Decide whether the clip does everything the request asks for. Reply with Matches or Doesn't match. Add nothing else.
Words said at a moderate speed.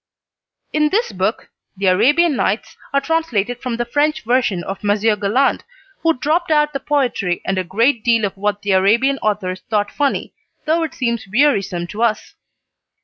Matches